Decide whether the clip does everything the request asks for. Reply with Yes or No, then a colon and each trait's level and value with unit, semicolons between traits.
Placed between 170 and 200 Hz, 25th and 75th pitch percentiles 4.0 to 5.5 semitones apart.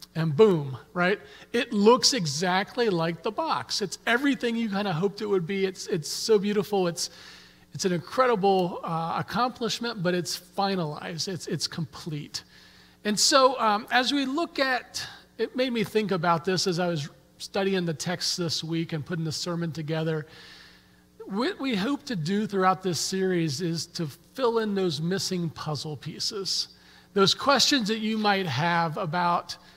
Yes: medium, 185 Hz; average, 4.6 semitones